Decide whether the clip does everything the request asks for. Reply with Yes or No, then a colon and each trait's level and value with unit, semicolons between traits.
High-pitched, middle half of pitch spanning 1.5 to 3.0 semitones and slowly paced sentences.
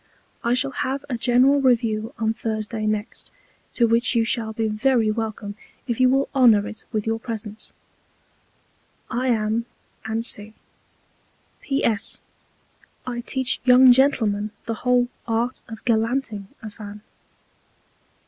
Yes: high, 230 Hz; narrow, 2.5 semitones; slow, 130 wpm